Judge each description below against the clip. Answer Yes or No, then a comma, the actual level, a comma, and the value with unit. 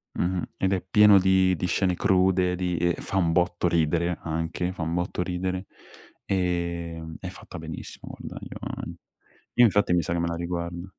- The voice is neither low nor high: No, very low, 90 Hz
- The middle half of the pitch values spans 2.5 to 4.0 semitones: No, narrow, 1.5 semitones